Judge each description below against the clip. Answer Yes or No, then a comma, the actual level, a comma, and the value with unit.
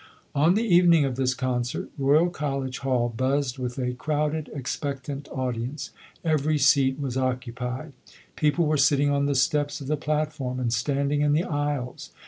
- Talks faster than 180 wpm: No, average, 160 wpm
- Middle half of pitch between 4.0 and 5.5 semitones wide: No, narrow, 2.6 semitones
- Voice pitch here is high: No, medium, 140 Hz